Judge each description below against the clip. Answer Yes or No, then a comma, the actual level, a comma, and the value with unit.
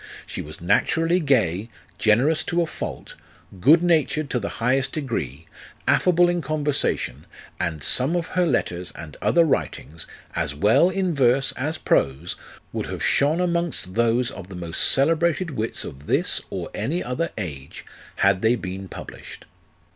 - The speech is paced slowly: No, average, 155 wpm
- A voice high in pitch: No, low, 125 Hz